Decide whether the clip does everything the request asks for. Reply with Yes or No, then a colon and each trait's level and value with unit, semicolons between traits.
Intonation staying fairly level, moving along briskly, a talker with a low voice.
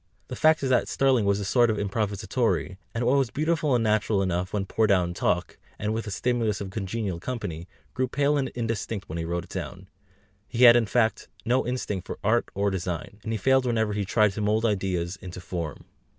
No: average, 4.1 semitones; fast, 220 wpm; low, 105 Hz